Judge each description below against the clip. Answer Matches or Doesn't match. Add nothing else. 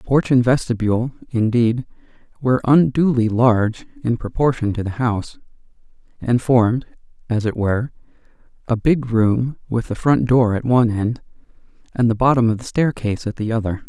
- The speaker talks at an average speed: Matches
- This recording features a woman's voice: Doesn't match